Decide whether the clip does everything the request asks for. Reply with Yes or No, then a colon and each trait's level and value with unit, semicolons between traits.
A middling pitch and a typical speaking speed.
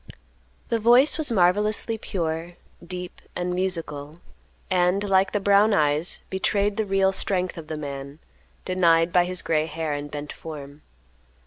Yes: medium, 180 Hz; average, 145 wpm